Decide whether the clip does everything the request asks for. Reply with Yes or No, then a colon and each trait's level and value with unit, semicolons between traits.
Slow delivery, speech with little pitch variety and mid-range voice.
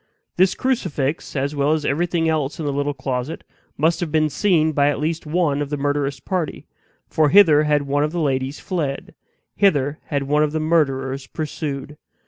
No: average, 185 wpm; narrow, 2.3 semitones; medium, 150 Hz